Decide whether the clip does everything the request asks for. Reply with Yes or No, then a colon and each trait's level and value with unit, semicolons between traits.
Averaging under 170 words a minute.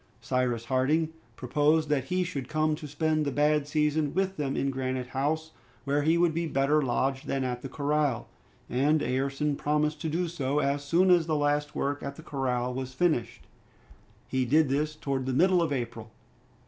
No: average, 185 wpm